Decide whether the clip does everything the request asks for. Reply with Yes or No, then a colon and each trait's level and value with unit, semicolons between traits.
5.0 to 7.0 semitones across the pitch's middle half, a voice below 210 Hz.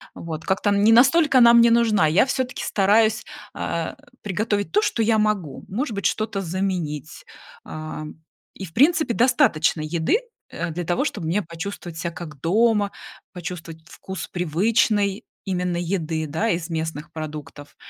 Yes: average, 5.3 semitones; high, 190 Hz